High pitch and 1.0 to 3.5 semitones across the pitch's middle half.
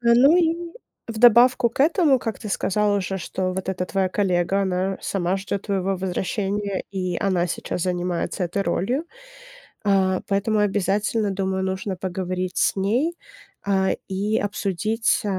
Yes: high, 195 Hz; narrow, 2.4 semitones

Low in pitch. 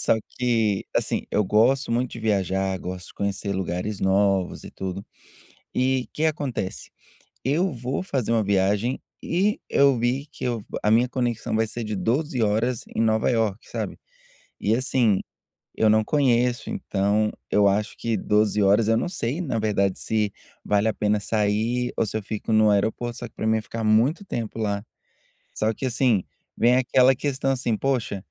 Yes: low, 110 Hz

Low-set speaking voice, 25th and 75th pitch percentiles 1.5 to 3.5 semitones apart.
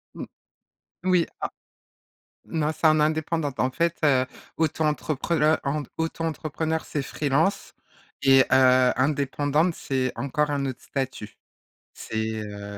No: medium, 145 Hz; average, 3.2 semitones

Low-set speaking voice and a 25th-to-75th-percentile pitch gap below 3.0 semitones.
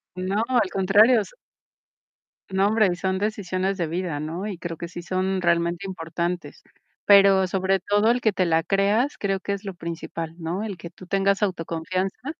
No: high, 190 Hz; narrow, 2.5 semitones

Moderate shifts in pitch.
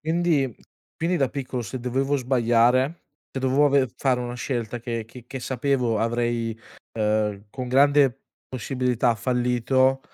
No: narrow, 2.3 semitones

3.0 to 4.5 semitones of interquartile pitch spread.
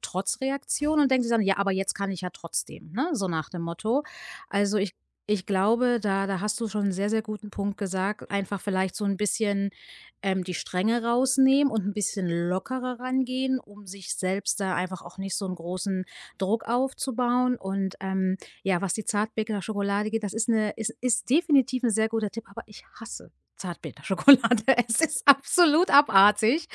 Yes: average, 4.1 semitones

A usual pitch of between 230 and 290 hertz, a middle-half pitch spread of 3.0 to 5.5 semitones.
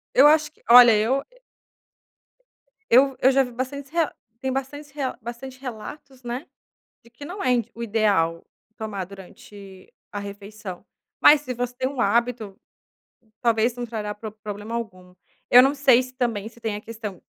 Yes: high, 235 Hz; average, 3.9 semitones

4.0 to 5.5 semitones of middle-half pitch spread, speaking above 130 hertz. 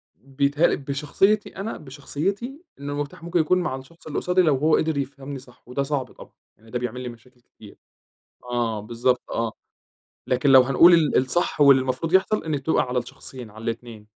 Yes: average, 4.3 semitones; medium, 140 Hz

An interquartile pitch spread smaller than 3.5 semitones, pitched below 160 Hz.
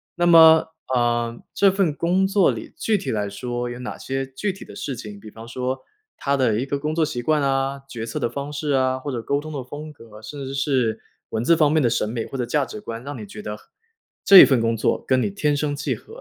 No: average, 4.3 semitones; low, 135 Hz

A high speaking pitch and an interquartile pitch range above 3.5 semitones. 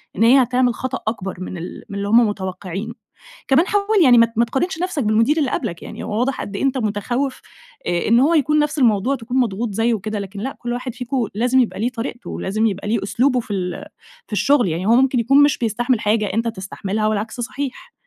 Yes: high, 230 Hz; average, 4.0 semitones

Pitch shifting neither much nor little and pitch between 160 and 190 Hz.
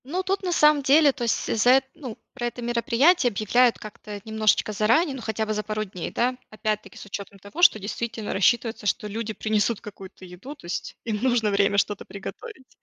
No: average, 3.5 semitones; high, 220 Hz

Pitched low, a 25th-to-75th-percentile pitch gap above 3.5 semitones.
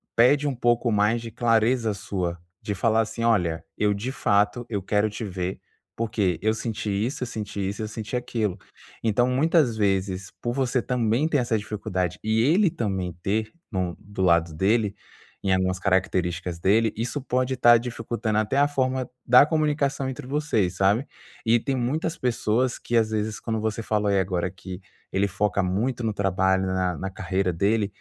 Yes: low, 110 Hz; average, 3.9 semitones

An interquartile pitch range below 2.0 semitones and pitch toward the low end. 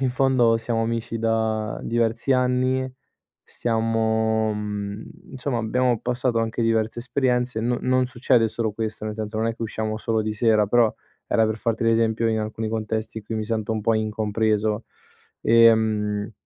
Yes: narrow, 1.4 semitones; low, 115 Hz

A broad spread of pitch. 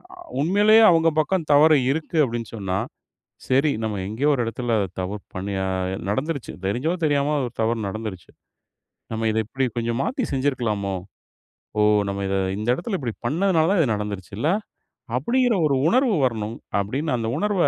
Yes: wide, 6.8 semitones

